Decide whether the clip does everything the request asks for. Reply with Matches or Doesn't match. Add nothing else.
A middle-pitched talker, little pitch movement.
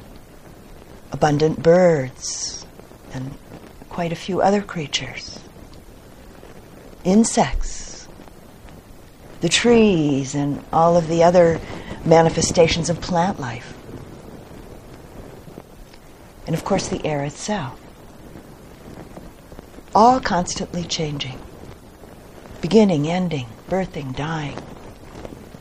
Doesn't match